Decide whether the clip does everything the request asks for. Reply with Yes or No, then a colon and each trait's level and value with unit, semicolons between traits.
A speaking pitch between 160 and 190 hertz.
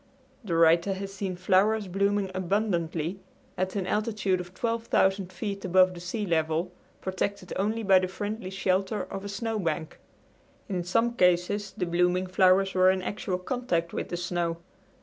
Yes: medium, 185 Hz